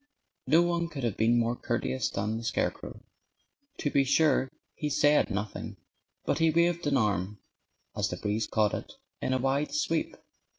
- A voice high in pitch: No, low, 130 Hz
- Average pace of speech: Yes, average, 170 wpm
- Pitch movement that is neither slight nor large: No, wide, 5.8 semitones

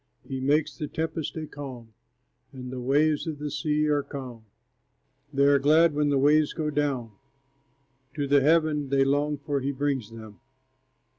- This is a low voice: No, medium, 145 Hz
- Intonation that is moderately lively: No, narrow, 2.0 semitones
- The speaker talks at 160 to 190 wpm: Yes, average, 165 wpm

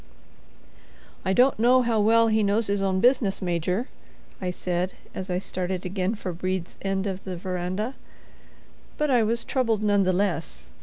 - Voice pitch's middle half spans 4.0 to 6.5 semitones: No, average, 3.4 semitones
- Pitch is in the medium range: No, high, 195 Hz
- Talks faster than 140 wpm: Yes, average, 165 wpm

